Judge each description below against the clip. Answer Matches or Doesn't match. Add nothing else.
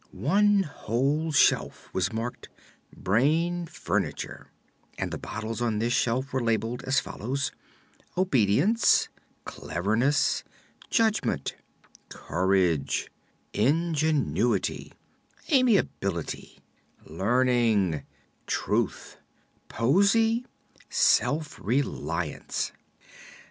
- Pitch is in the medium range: Doesn't match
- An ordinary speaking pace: Doesn't match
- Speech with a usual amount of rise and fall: Doesn't match